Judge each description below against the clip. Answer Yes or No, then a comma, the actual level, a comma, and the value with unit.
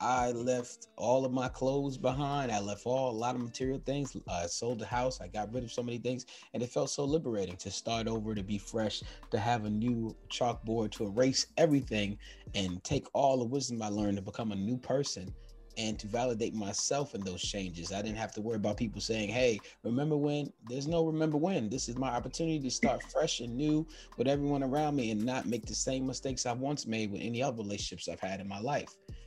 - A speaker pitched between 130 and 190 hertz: No, low, 120 Hz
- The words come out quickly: Yes, fast, 225 wpm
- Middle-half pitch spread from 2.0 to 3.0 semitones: No, average, 3.8 semitones